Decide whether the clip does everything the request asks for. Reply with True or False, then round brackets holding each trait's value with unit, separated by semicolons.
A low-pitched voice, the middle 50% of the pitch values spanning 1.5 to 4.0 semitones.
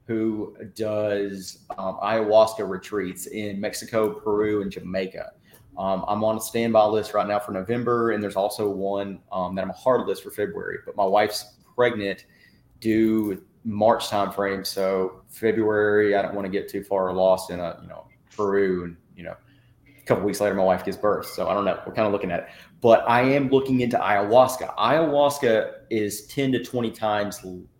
True (105 Hz; 2.8 semitones)